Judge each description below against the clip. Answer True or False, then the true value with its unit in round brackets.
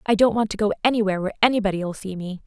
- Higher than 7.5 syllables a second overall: True (8.0 syllables/s)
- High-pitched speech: True (205 Hz)